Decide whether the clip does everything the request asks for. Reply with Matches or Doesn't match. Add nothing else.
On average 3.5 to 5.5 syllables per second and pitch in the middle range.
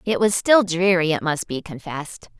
Matches